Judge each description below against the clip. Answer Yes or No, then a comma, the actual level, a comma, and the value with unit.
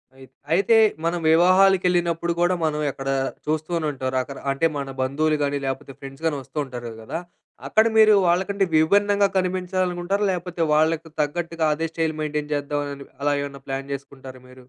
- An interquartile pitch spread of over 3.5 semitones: Yes, average, 4.2 semitones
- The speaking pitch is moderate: Yes, medium, 155 Hz